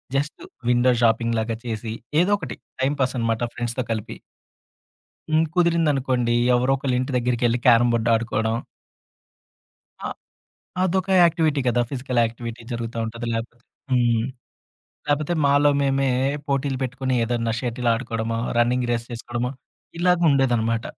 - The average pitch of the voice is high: No, low, 120 Hz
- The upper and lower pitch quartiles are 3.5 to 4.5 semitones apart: No, average, 2.9 semitones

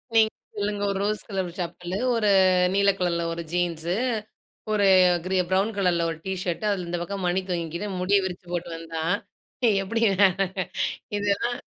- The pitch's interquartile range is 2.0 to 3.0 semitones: Yes, average, 2.7 semitones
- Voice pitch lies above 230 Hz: No, medium, 185 Hz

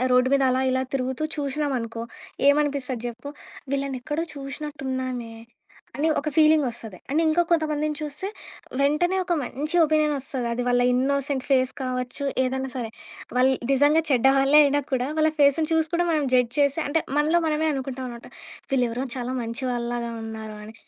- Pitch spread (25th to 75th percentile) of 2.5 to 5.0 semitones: Yes, average, 3.1 semitones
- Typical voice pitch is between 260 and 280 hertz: Yes, very high, 270 Hz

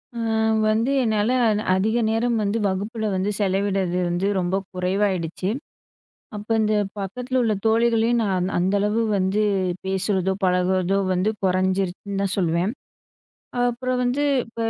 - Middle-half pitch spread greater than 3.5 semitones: No, average, 3.1 semitones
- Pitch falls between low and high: No, high, 200 Hz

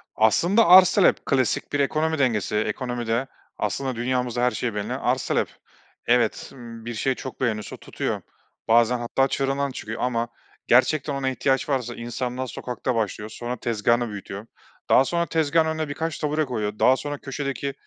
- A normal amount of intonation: Yes, average, 3.2 semitones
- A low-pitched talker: Yes, low, 125 Hz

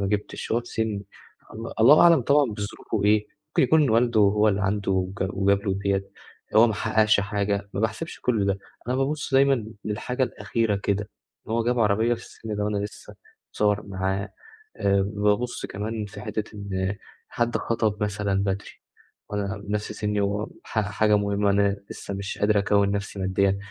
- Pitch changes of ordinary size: No, narrow, 1.9 semitones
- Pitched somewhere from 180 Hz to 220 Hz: No, low, 105 Hz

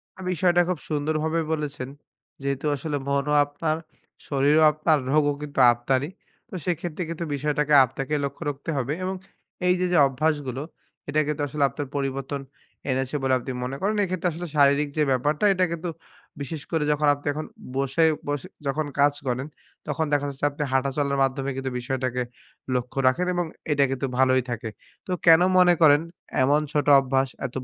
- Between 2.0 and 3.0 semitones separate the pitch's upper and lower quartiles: Yes, narrow, 2.6 semitones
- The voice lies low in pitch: No, medium, 145 Hz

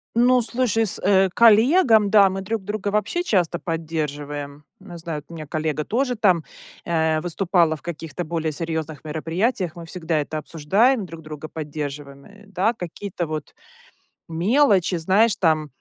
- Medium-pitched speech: Yes, medium, 170 Hz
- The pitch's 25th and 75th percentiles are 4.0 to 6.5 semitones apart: Yes, average, 4.9 semitones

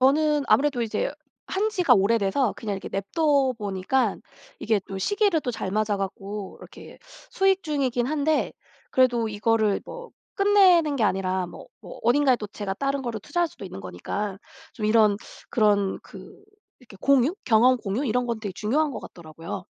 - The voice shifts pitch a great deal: Yes, wide, 6.1 semitones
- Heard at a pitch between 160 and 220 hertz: No, high, 235 Hz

